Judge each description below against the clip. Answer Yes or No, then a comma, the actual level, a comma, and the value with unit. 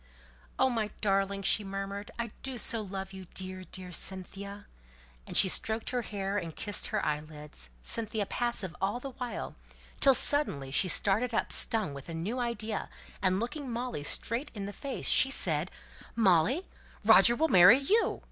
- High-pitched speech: Yes, high, 205 Hz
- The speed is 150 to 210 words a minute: Yes, average, 165 wpm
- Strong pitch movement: No, average, 4.2 semitones